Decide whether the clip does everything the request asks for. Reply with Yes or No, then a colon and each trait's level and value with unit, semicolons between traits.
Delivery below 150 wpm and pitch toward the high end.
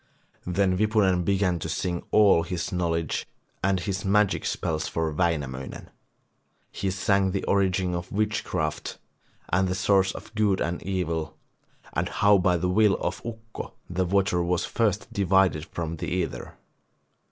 No: average, 140 wpm; very low, 95 Hz